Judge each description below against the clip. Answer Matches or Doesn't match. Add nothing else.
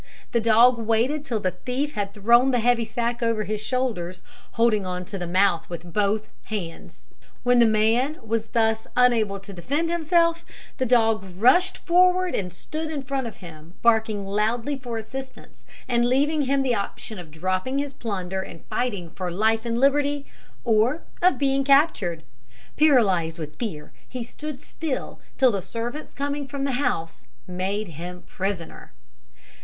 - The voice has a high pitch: Matches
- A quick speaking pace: Doesn't match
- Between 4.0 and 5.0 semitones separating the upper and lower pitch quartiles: Doesn't match